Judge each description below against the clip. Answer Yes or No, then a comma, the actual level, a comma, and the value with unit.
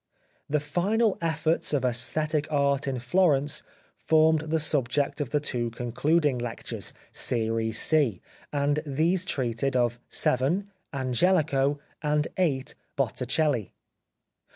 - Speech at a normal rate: No, slow, 115 wpm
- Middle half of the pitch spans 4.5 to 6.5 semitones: No, average, 3.9 semitones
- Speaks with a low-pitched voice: No, medium, 145 Hz